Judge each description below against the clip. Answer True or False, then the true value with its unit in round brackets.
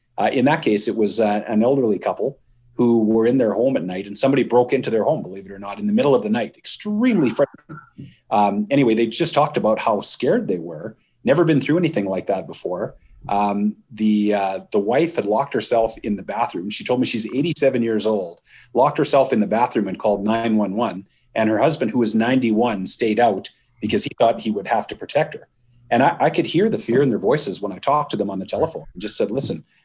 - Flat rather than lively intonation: False (4.3 semitones)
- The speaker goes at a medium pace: False (235 wpm)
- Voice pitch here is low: True (115 Hz)